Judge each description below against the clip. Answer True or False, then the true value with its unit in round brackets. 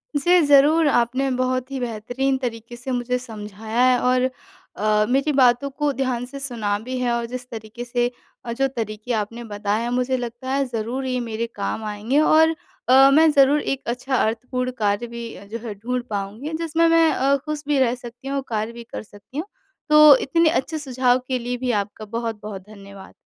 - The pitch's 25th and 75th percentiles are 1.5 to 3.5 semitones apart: True (3.2 semitones)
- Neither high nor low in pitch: False (245 Hz)